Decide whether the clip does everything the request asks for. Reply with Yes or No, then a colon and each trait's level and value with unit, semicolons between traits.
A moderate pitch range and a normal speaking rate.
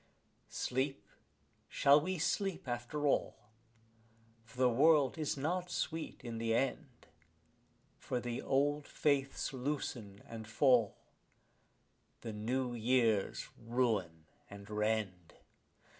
No: average, 4.2 semitones; slow, 105 wpm